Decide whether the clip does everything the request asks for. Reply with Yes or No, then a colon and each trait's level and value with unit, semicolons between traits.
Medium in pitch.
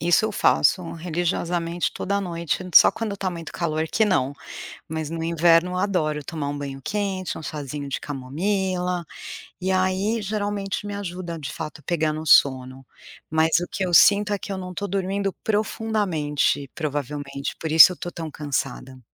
Yes: medium, 170 Hz